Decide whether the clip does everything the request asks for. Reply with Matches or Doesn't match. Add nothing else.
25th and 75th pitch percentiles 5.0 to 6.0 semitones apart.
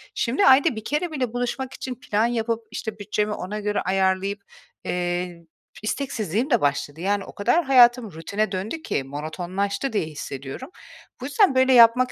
Matches